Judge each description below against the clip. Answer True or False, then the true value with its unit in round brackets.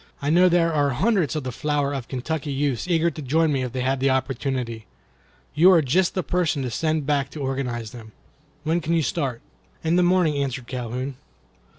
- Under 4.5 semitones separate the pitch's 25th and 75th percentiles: True (4.0 semitones)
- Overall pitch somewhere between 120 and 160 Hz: True (140 Hz)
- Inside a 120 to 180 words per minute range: False (205 wpm)